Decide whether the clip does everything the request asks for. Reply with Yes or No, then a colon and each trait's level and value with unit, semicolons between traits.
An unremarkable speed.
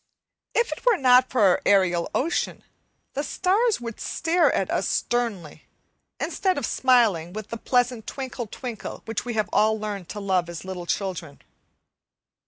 Yes: average, 160 wpm